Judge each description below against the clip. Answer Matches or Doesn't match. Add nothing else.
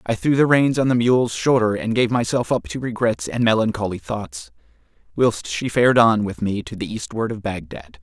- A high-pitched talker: Doesn't match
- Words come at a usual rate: Doesn't match